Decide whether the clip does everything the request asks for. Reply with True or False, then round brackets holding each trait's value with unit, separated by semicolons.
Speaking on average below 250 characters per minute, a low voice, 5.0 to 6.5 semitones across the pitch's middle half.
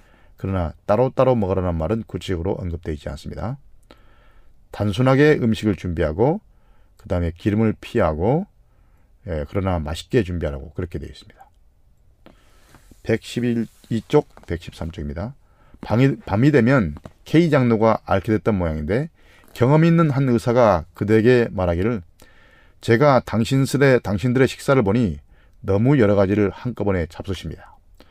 False (295 characters per minute; 105 Hz; 5.5 semitones)